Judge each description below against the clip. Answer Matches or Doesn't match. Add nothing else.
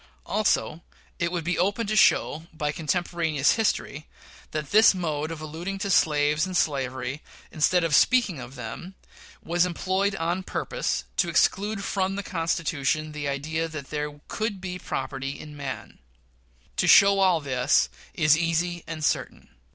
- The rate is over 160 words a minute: Doesn't match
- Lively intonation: Doesn't match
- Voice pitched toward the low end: Doesn't match